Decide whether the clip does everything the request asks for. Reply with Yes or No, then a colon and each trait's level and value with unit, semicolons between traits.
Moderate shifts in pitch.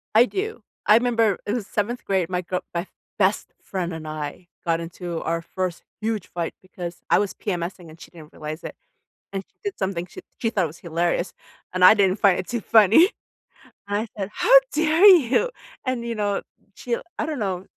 Yes: average, 4.8 semitones